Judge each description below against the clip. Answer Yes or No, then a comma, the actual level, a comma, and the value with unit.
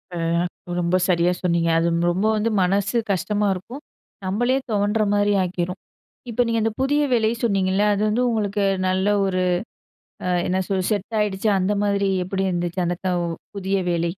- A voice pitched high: Yes, high, 195 Hz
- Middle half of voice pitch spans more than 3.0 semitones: No, narrow, 2.5 semitones